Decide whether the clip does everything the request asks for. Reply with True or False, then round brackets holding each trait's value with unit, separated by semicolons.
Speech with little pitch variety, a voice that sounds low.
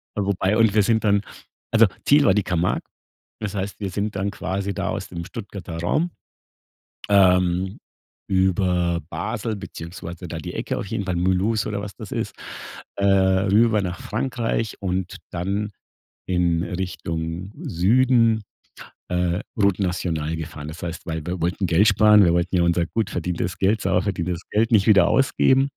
False (3.0 semitones; 95 Hz)